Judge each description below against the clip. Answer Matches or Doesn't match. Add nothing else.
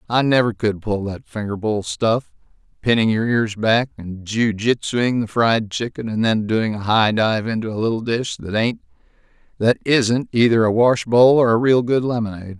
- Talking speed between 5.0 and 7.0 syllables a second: Doesn't match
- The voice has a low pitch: Matches